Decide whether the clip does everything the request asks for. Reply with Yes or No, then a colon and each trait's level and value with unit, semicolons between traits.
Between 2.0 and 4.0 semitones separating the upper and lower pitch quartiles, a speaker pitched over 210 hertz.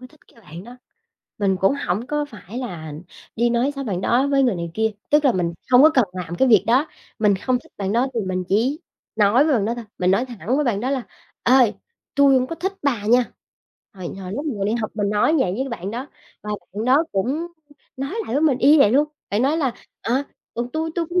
No: average, 5.3 semitones; high, 240 Hz